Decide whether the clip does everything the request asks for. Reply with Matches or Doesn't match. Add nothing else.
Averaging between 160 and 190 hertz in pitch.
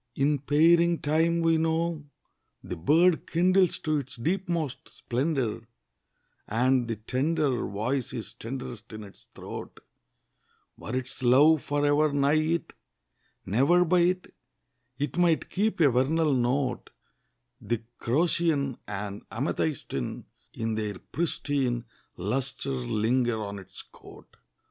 Doesn't match